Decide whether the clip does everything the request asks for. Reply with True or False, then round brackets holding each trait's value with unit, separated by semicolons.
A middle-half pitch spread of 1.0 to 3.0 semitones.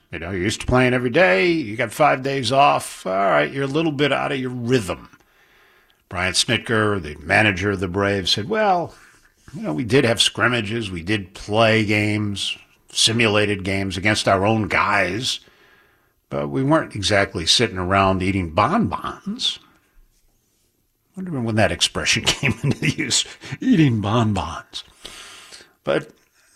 False (4.3 semitones)